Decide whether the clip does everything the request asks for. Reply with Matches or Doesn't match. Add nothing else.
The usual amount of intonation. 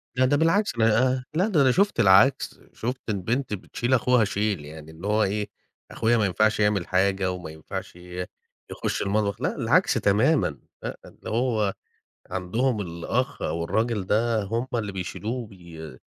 Matches